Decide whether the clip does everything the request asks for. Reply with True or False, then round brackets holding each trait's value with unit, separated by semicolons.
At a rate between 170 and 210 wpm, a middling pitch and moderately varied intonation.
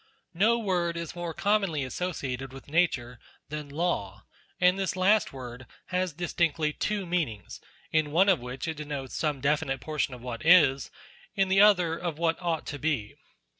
True (175 wpm; 160 Hz; 5.0 semitones)